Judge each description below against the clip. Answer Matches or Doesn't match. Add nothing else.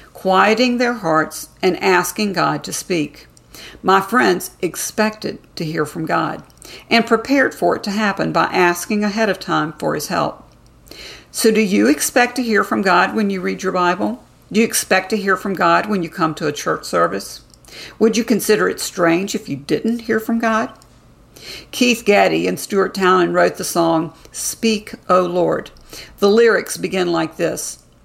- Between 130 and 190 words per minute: Matches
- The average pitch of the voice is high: Matches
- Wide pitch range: Doesn't match